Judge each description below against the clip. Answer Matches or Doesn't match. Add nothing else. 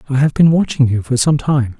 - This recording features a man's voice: Matches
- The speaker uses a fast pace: Matches